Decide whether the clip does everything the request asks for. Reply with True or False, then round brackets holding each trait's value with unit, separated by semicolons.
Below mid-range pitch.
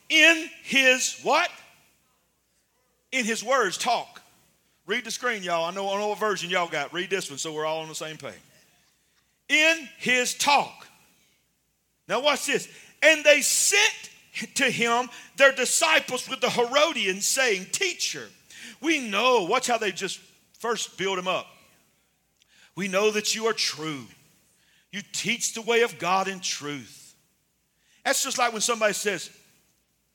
False (225 Hz)